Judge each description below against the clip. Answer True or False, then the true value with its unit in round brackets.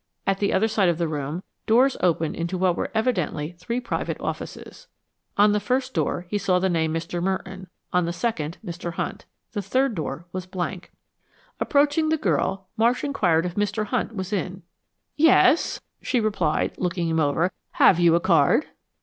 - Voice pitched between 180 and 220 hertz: True (185 Hz)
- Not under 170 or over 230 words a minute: True (175 wpm)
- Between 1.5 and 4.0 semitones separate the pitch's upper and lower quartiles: False (4.4 semitones)